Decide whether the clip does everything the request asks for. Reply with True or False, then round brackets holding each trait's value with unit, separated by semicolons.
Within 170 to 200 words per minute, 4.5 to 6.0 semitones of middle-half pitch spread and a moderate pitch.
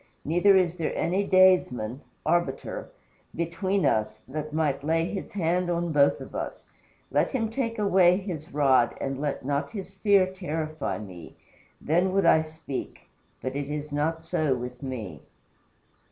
False (155 wpm; 4.8 semitones; 160 Hz)